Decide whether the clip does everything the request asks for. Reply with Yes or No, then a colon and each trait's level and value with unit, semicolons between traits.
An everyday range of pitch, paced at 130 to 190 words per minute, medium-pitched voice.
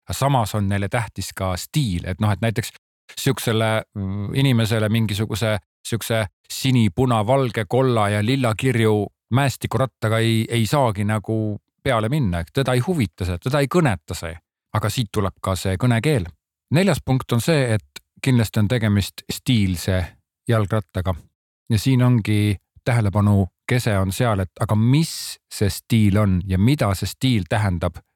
No: average, 4.0 semitones; average, 145 wpm; low, 110 Hz